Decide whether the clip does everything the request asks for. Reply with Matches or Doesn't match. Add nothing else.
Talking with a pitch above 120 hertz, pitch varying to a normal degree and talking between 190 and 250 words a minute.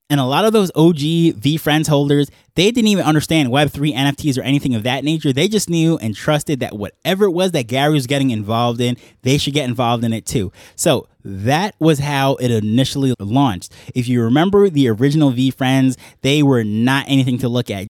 Matches